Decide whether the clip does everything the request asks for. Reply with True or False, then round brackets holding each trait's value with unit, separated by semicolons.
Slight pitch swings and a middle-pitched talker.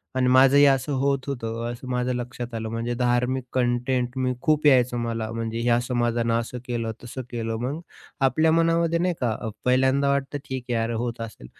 False (2.2 semitones; 125 Hz)